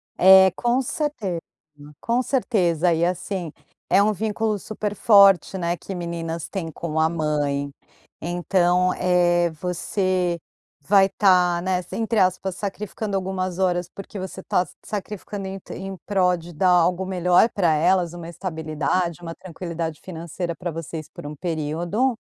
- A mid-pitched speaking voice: Yes, medium, 180 Hz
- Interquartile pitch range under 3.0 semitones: Yes, narrow, 2.4 semitones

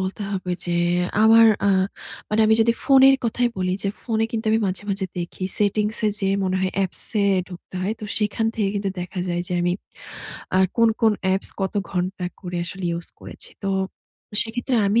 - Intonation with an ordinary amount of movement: Yes, average, 3.1 semitones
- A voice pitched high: Yes, high, 200 Hz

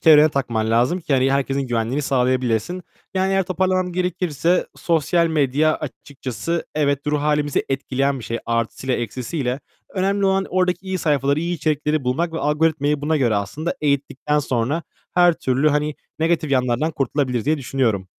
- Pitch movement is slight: No, average, 4.2 semitones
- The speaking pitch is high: No, medium, 145 Hz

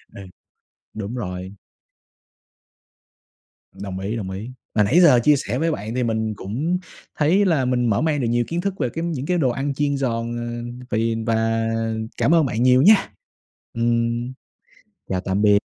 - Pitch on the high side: No, low, 120 Hz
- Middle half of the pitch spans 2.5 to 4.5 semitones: No, average, 4.9 semitones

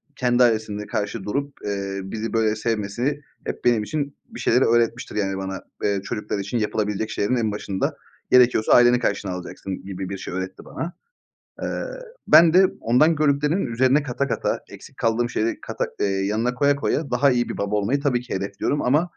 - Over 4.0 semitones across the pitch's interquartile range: Yes, average, 4.4 semitones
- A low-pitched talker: Yes, low, 115 Hz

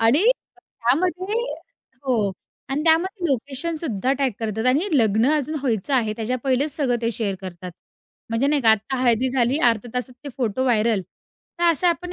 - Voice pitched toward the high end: Yes, very high, 255 Hz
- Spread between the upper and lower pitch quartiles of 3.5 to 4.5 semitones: No, average, 5.0 semitones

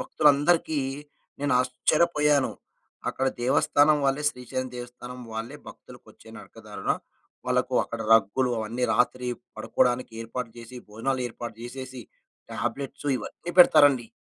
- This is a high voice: No, low, 125 Hz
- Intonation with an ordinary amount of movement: Yes, average, 3.0 semitones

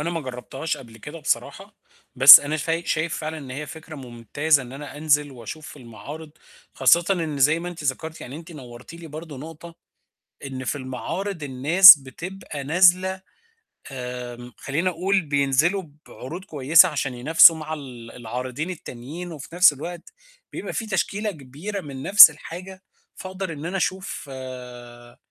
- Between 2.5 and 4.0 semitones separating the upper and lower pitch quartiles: No, average, 4.5 semitones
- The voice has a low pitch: No, medium, 150 Hz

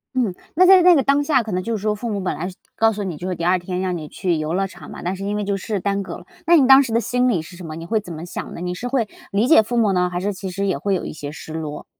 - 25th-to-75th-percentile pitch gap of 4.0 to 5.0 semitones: Yes, average, 4.4 semitones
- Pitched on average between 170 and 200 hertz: Yes, high, 195 Hz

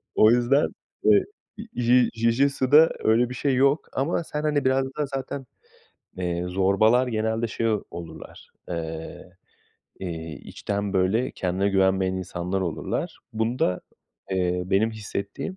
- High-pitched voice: No, low, 110 Hz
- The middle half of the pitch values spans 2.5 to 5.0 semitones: No, wide, 5.5 semitones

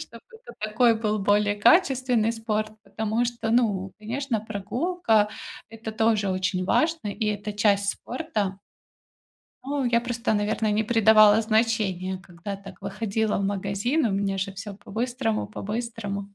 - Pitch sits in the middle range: No, high, 215 Hz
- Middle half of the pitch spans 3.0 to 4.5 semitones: No, narrow, 2.5 semitones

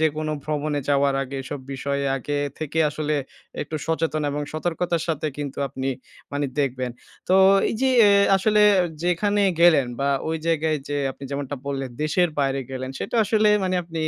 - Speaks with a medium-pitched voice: Yes, medium, 150 Hz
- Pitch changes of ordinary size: Yes, average, 3.0 semitones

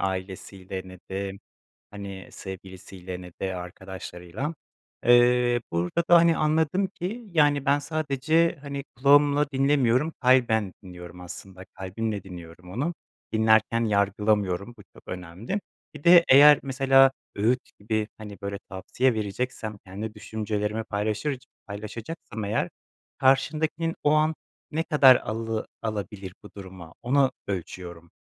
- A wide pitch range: Yes, wide, 6.6 semitones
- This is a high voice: No, low, 110 Hz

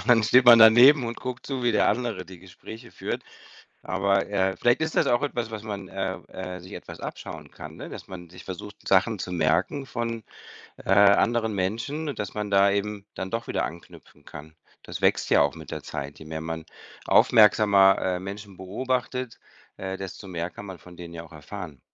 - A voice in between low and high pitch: No, low, 100 Hz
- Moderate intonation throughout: Yes, average, 4.2 semitones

